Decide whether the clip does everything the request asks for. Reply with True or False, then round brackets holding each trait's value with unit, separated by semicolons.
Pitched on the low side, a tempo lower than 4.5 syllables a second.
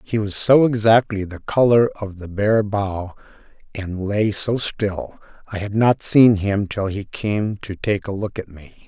True (105 Hz; 4.0 syllables/s)